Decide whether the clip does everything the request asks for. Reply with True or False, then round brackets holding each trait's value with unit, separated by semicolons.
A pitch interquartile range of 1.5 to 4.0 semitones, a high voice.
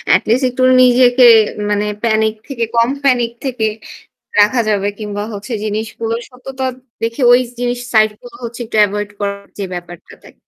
True (2.9 semitones; 230 Hz)